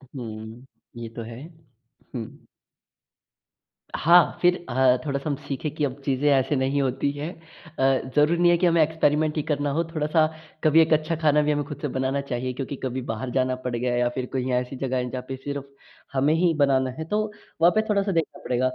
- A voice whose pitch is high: No, medium, 140 Hz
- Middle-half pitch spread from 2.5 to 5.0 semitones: Yes, average, 3.3 semitones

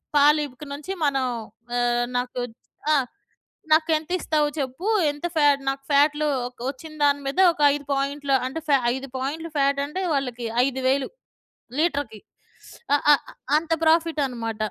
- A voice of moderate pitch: No, very high, 285 Hz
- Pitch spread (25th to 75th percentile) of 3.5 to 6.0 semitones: No, narrow, 2.5 semitones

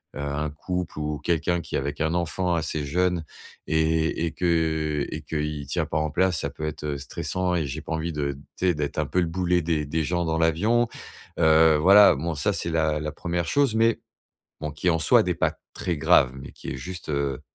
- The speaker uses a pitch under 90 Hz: Yes, very low, 80 Hz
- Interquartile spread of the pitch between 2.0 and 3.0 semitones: Yes, narrow, 2.6 semitones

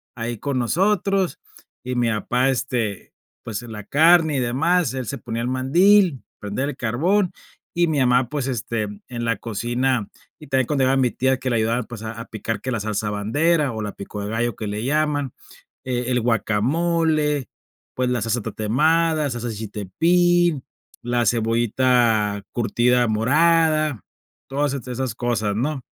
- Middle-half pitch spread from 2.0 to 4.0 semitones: No, average, 4.6 semitones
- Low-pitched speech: Yes, low, 125 Hz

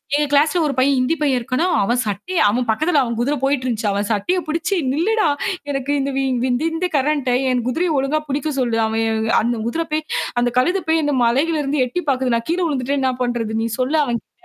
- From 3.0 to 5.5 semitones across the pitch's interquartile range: Yes, average, 4.3 semitones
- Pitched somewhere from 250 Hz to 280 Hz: Yes, very high, 270 Hz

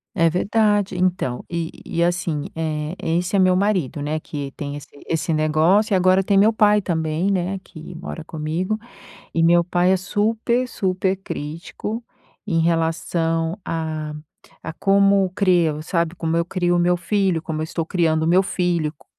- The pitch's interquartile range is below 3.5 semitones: Yes, average, 3.0 semitones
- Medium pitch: Yes, medium, 175 Hz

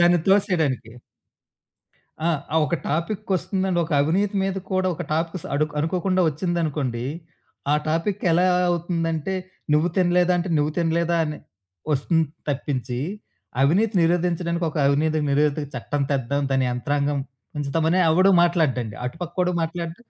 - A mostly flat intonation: No, average, 3.5 semitones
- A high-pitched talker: No, medium, 165 Hz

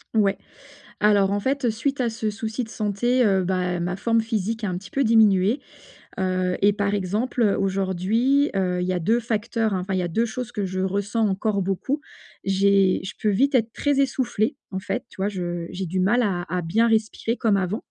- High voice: Yes, high, 205 Hz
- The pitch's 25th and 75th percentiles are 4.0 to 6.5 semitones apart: No, average, 3.4 semitones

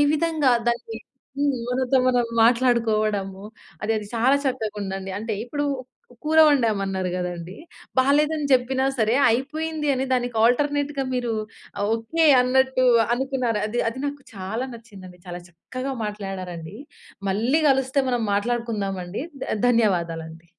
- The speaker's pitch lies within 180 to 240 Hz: Yes, high, 235 Hz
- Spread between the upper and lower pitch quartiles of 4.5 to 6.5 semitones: Yes, average, 5.0 semitones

